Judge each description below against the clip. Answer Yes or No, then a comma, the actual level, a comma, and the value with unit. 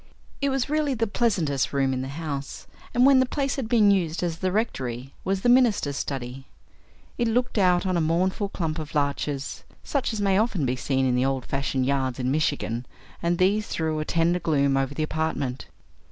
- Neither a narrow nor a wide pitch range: No, wide, 7.2 semitones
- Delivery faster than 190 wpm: Yes, average, 200 wpm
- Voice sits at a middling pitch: Yes, medium, 160 Hz